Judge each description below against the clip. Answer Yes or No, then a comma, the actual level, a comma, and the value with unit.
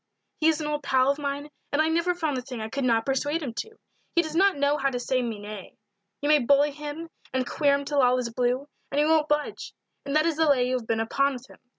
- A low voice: No, very high, 280 Hz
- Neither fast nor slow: No, fast, 275 wpm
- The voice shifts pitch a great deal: No, average, 3.0 semitones